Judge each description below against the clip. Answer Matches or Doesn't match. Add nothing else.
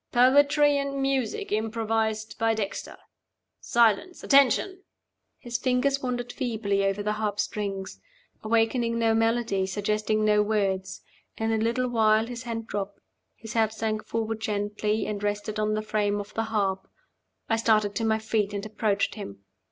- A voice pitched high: Matches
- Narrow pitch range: Matches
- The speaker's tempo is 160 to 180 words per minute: Doesn't match